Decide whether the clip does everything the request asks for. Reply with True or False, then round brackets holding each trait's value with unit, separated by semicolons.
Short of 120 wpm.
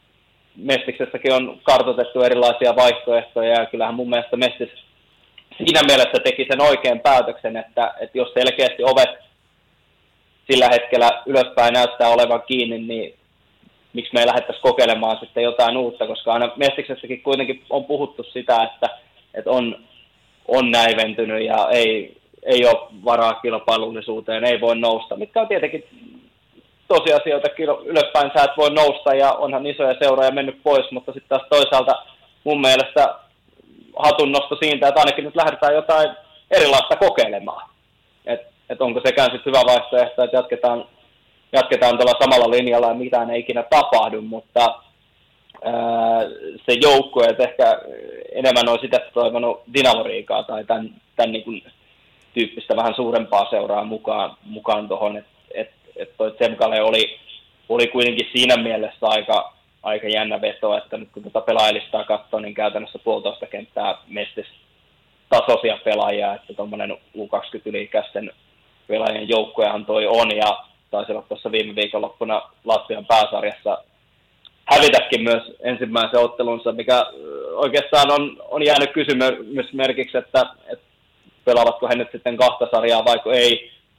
False (135 wpm)